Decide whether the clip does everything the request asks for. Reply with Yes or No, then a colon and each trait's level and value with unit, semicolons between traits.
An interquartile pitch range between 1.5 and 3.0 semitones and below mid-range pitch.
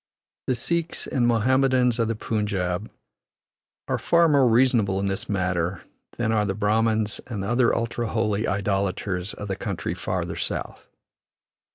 No: average, 3.5 semitones; low, 110 Hz